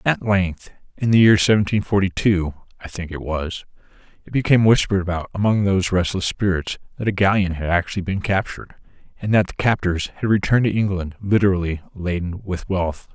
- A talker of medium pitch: No, very low, 95 Hz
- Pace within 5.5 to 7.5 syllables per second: Yes, 5.8 syllables/s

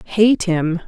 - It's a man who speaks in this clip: No, female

